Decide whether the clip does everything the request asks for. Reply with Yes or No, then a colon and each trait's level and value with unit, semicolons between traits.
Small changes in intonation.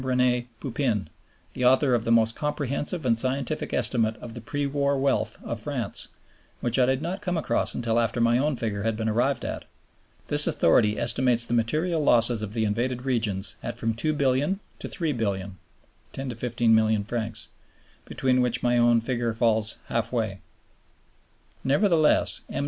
No: average, 3.1 semitones